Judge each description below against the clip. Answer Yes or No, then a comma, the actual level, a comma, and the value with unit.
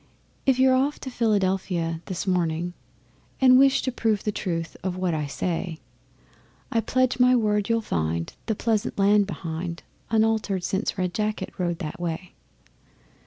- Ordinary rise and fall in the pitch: Yes, average, 4.8 semitones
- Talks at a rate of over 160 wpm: No, average, 155 wpm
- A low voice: No, high, 195 Hz